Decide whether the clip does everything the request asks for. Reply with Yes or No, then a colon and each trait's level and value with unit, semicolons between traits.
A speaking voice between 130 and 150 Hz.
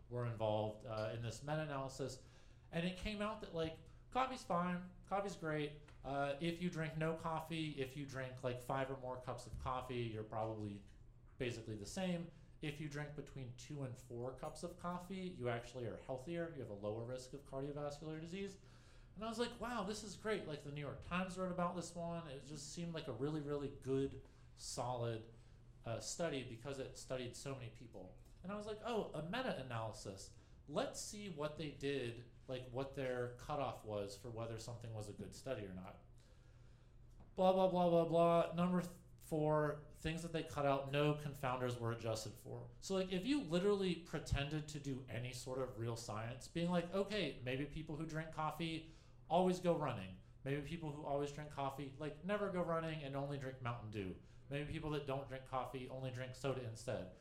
Yes: medium, 140 Hz